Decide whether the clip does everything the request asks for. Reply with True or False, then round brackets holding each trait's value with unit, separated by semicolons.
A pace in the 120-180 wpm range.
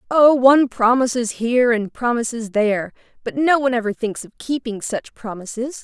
True (165 wpm)